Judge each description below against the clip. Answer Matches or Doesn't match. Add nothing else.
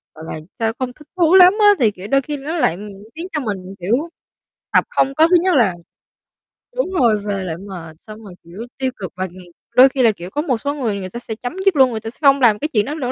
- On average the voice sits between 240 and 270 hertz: Matches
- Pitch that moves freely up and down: Matches